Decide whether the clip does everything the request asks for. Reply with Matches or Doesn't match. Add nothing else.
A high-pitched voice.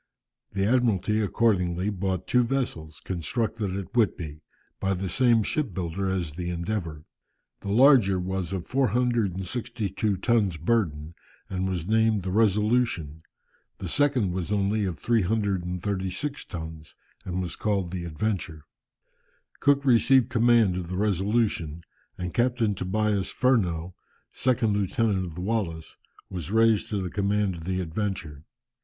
Doesn't match